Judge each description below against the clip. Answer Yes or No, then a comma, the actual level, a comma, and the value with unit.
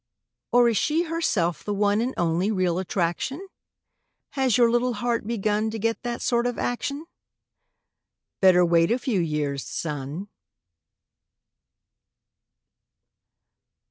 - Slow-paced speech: Yes, slow, 115 wpm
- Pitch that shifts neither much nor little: No, wide, 5.7 semitones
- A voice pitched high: Yes, high, 215 Hz